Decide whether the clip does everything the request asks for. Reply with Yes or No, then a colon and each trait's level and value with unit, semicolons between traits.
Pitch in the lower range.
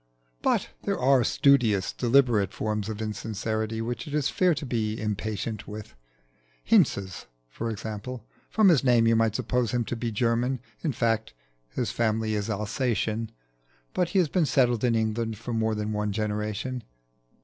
Yes: low, 115 Hz